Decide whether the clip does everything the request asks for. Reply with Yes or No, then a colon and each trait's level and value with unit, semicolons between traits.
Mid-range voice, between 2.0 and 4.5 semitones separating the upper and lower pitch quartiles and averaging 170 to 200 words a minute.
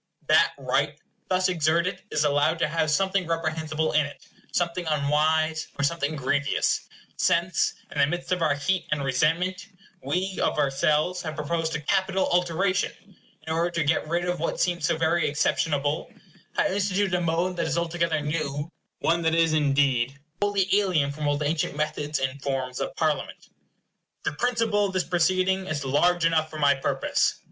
Yes: medium, 160 Hz; average, 3.2 semitones; average, 175 wpm